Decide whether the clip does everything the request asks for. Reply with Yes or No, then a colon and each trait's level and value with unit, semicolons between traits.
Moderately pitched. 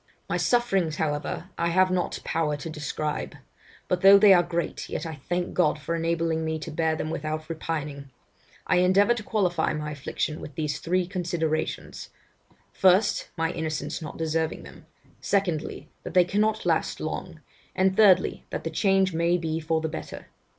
Yes: medium, 165 Hz